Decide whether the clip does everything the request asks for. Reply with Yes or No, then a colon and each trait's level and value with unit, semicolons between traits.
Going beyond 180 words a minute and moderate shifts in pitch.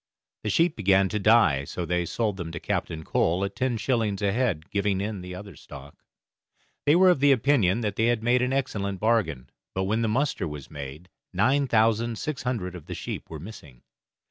Yes: fast, 205 wpm; average, 4.9 semitones